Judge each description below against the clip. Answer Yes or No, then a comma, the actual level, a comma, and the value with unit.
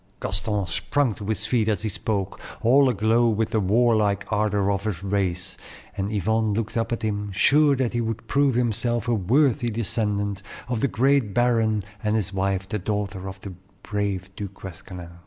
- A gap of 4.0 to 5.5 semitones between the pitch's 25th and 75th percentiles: No, average, 3.0 semitones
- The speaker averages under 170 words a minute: No, average, 180 wpm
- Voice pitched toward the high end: No, low, 105 Hz